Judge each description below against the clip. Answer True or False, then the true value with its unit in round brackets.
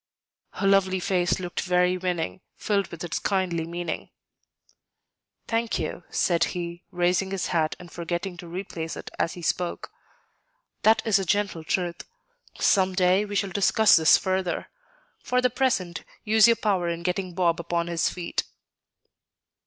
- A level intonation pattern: True (2.3 semitones)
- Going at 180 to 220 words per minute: False (155 wpm)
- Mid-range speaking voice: True (180 Hz)